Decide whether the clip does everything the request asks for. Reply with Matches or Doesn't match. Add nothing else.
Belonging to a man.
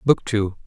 Matches